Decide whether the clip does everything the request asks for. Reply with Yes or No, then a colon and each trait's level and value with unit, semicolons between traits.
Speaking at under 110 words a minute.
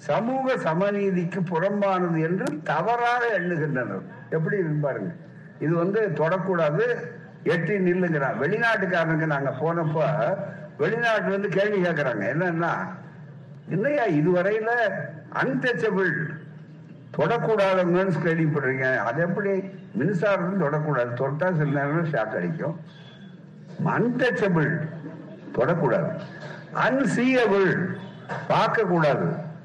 Yes: slow, 75 wpm